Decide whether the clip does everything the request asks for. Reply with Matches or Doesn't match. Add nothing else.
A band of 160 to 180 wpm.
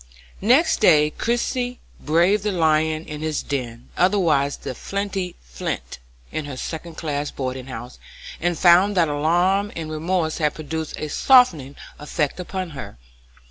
Doesn't match